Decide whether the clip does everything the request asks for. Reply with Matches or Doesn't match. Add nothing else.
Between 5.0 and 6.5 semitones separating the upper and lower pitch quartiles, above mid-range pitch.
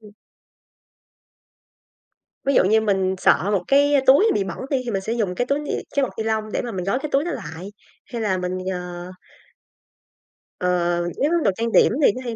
Matches